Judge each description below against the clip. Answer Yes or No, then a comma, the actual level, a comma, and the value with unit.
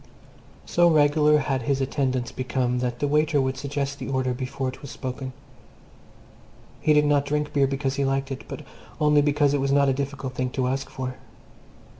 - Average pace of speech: Yes, average, 190 wpm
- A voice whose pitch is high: No, low, 135 Hz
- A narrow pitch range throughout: Yes, narrow, 1.9 semitones